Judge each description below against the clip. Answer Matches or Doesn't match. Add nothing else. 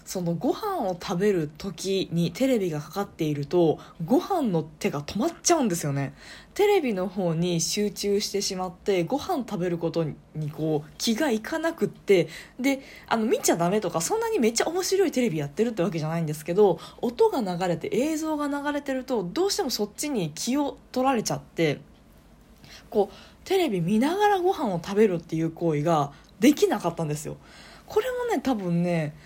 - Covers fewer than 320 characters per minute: Doesn't match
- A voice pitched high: Matches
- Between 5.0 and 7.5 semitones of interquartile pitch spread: Doesn't match